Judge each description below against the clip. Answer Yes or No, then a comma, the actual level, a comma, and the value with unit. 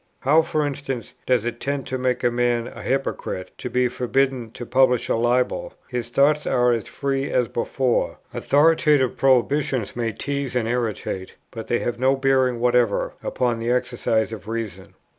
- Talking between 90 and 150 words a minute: No, average, 170 wpm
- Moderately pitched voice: No, low, 125 Hz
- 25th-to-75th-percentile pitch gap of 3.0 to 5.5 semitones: No, narrow, 2.4 semitones